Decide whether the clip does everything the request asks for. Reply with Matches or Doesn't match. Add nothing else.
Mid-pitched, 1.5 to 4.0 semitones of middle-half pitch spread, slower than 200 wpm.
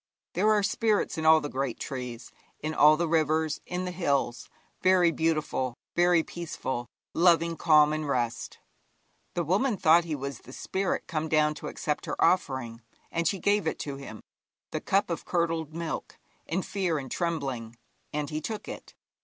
Matches